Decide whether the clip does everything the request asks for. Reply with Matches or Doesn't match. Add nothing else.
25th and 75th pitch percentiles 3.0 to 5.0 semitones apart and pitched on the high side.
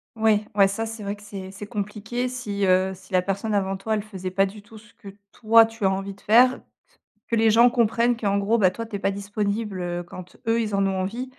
Doesn't match